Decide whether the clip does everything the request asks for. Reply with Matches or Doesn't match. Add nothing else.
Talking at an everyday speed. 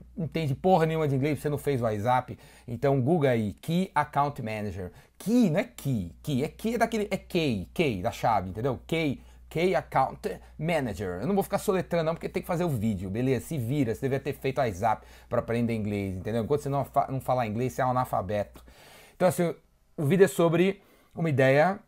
Doesn't match